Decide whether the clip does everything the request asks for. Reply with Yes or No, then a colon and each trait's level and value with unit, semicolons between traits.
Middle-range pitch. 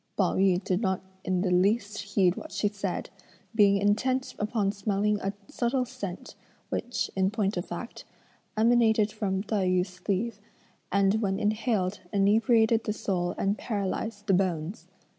No: high, 205 Hz